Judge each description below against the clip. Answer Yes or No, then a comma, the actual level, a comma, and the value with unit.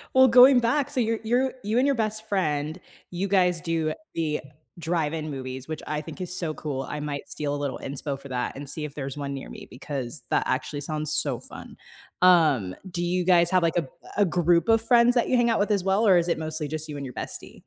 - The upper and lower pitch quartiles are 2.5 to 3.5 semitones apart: No, wide, 5.6 semitones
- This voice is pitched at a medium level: Yes, medium, 165 Hz